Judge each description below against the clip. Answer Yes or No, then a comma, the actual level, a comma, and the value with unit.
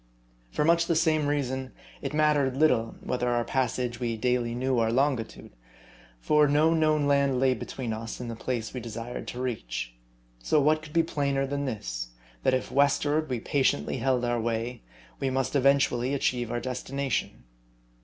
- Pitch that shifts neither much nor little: Yes, average, 3.1 semitones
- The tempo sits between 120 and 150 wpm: No, average, 175 wpm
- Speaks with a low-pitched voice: Yes, low, 130 Hz